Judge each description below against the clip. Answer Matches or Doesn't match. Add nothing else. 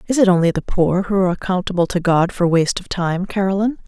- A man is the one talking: Doesn't match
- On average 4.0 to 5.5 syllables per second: Doesn't match